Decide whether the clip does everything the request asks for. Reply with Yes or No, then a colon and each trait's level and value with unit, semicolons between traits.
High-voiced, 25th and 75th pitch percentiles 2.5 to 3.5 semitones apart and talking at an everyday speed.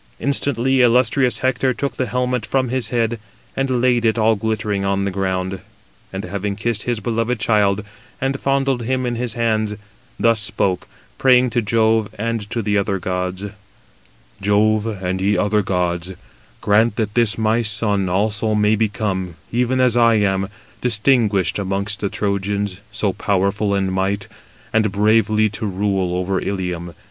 No: low, 105 Hz; average, 3.0 semitones; average, 155 wpm